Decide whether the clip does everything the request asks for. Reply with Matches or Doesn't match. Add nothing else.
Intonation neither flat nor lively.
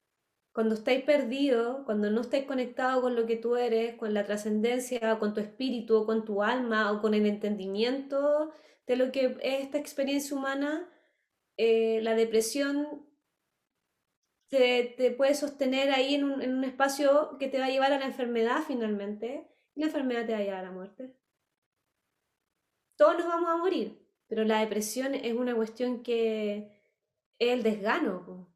Matches